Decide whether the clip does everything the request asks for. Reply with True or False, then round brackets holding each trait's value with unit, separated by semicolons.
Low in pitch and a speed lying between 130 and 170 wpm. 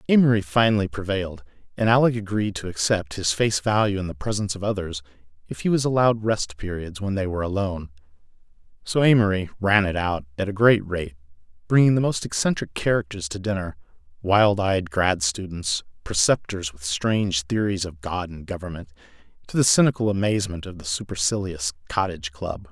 True (95 Hz; 165 wpm)